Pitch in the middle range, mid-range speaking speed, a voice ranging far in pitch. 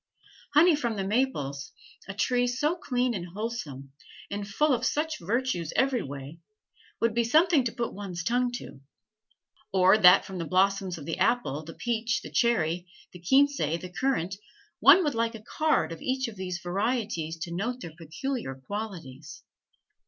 No: high, 205 Hz; average, 165 wpm; wide, 6.4 semitones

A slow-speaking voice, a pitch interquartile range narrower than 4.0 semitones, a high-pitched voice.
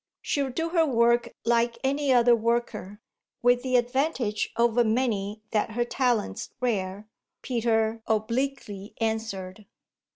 Yes: slow, 120 wpm; narrow, 2.5 semitones; high, 235 Hz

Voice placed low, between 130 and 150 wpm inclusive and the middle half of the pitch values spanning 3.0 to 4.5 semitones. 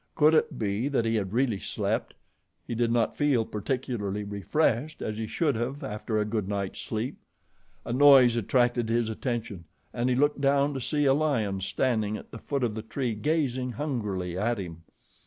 No: low, 120 Hz; average, 180 wpm; average, 4.2 semitones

